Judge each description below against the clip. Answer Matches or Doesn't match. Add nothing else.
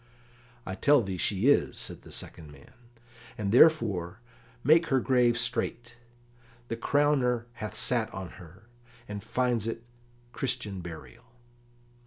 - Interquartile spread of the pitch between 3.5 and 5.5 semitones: Matches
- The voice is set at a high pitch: Doesn't match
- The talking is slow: Matches